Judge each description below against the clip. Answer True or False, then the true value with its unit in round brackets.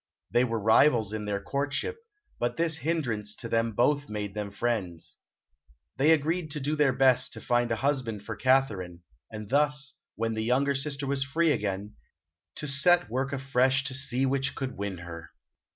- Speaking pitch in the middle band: False (130 Hz)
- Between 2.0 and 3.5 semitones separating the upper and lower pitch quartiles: False (4.6 semitones)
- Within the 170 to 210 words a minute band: True (180 wpm)